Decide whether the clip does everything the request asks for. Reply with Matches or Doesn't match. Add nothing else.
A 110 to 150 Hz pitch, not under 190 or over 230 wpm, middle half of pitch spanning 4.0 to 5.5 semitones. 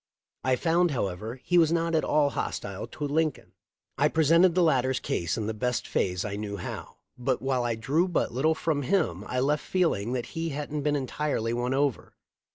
Matches